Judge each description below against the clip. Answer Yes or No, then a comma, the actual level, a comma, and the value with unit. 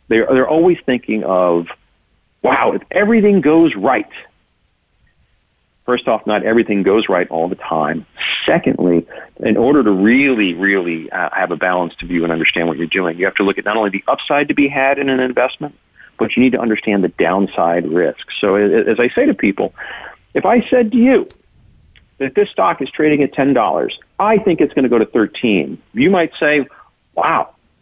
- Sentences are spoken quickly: No, average, 190 wpm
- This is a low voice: Yes, low, 115 Hz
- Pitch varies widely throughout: Yes, wide, 8.6 semitones